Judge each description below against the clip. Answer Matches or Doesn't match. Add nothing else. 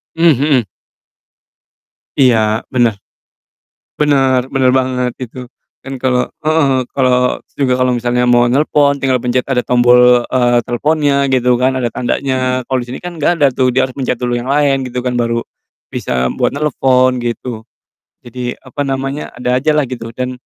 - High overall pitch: Doesn't match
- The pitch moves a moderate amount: Doesn't match